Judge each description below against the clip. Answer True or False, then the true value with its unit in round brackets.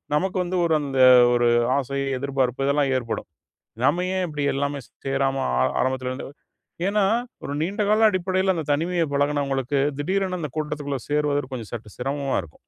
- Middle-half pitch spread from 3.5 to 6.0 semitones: True (4.3 semitones)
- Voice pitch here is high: False (145 Hz)